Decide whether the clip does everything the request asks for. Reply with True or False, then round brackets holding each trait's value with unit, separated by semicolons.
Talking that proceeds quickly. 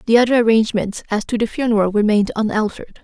False (180 wpm)